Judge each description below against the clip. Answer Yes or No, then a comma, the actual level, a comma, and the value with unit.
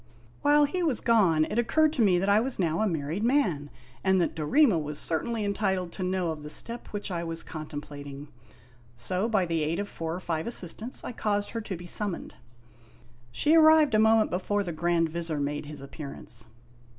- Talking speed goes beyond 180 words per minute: Yes, average, 200 wpm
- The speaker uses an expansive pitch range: Yes, wide, 5.7 semitones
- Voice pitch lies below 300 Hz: Yes, medium, 185 Hz